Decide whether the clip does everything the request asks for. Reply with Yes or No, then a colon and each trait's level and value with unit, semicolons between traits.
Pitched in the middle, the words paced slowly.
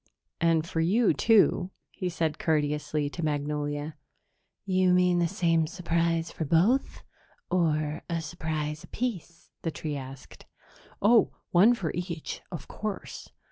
Yes: medium, 165 Hz; slow, 130 wpm